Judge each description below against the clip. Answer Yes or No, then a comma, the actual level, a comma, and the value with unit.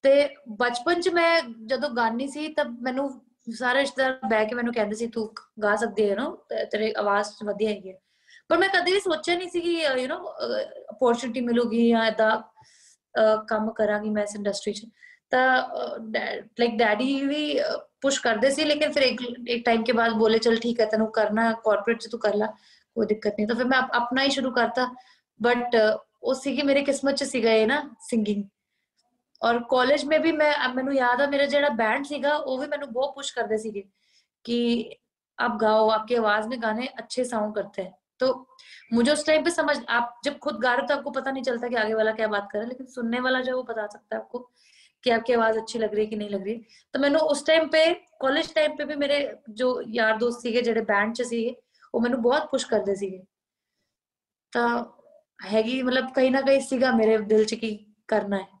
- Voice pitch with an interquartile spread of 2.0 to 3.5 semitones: No, average, 4.0 semitones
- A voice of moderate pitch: No, high, 240 Hz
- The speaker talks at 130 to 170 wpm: Yes, average, 160 wpm